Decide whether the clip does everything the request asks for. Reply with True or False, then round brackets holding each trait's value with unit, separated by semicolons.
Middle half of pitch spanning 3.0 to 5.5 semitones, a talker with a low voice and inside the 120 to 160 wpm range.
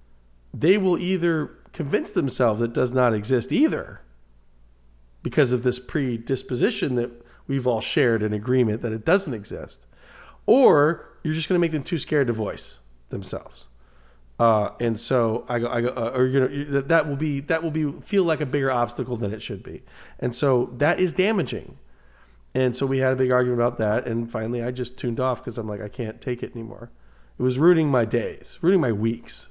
False (3.9 semitones; 125 Hz; 200 wpm)